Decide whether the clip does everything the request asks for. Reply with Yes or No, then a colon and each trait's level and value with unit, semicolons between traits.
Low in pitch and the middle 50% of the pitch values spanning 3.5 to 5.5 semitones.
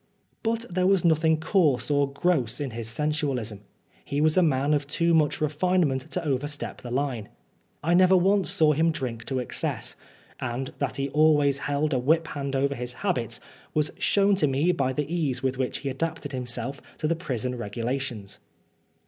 No: medium, 145 Hz; average, 3.8 semitones